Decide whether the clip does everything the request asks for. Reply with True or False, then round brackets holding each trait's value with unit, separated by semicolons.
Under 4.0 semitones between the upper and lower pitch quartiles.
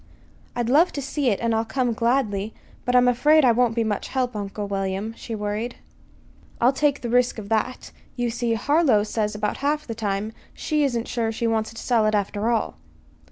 True (2.8 semitones)